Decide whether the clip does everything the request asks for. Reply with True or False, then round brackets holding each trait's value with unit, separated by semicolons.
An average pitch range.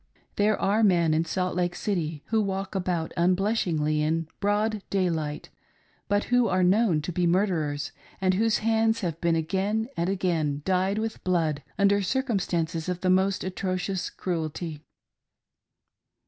True (3.6 semitones)